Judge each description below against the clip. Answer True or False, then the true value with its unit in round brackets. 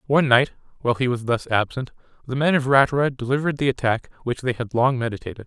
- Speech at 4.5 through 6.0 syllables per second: False (6.8 syllables/s)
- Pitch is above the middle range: False (130 Hz)